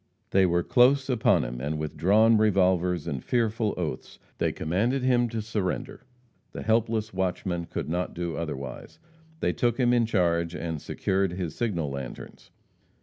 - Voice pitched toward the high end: No, very low, 95 Hz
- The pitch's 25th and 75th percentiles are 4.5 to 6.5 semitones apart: Yes, average, 5.1 semitones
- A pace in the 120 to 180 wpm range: Yes, average, 155 wpm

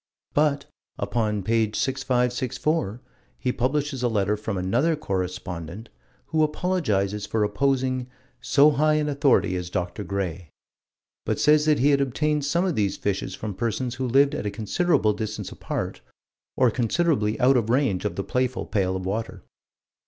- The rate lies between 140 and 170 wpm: Yes, average, 155 wpm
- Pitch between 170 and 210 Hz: No, low, 120 Hz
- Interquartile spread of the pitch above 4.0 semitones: Yes, wide, 5.5 semitones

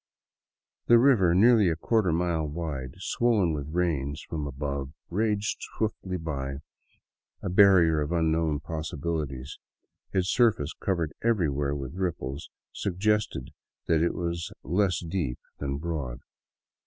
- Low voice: Yes, very low, 85 Hz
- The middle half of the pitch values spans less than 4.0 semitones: No, average, 4.7 semitones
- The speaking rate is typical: No, slow, 120 wpm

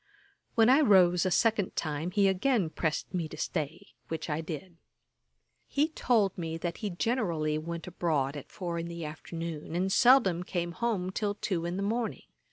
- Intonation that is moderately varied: Yes, average, 3.9 semitones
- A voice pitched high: No, medium, 175 Hz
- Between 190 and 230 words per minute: No, average, 175 wpm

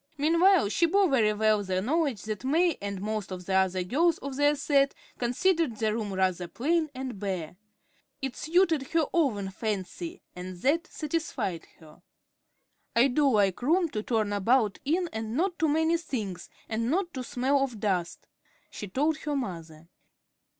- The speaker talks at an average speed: Yes, average, 165 wpm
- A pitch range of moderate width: No, wide, 7.7 semitones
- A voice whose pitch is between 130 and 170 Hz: No, high, 245 Hz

